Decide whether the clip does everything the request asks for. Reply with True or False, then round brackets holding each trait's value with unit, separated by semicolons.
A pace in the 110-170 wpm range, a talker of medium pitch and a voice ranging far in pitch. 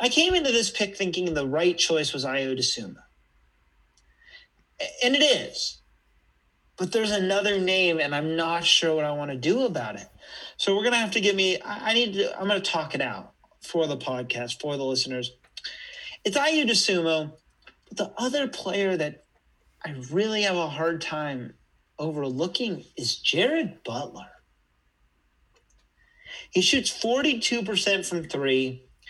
True (150 wpm; 165 Hz; 8.0 semitones)